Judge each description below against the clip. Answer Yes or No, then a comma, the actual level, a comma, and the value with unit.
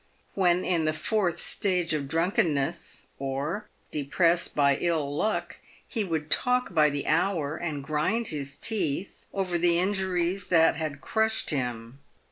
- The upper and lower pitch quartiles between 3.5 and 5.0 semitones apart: Yes, average, 4.2 semitones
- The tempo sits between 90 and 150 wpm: Yes, average, 140 wpm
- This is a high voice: No, medium, 165 Hz